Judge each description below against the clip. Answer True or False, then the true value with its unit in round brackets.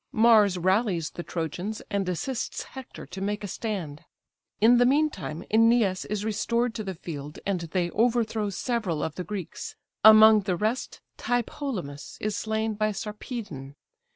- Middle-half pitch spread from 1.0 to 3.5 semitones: False (4.0 semitones)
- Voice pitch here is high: True (210 Hz)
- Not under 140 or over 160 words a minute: True (150 wpm)